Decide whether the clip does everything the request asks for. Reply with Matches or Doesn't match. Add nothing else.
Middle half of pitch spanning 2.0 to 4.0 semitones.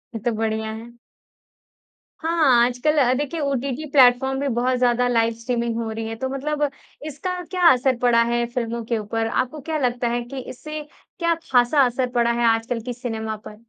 Matches